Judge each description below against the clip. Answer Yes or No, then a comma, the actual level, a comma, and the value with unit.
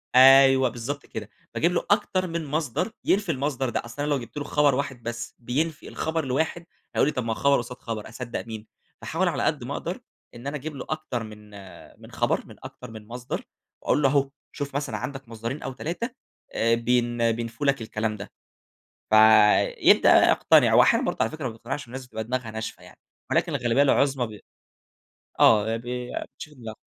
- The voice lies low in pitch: Yes, low, 130 Hz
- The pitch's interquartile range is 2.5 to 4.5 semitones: Yes, average, 3.7 semitones